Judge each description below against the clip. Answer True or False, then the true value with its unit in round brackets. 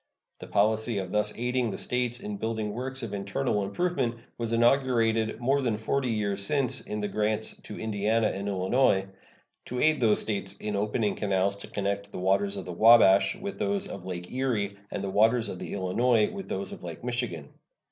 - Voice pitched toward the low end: True (110 Hz)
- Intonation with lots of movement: False (3.5 semitones)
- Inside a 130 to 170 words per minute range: False (190 wpm)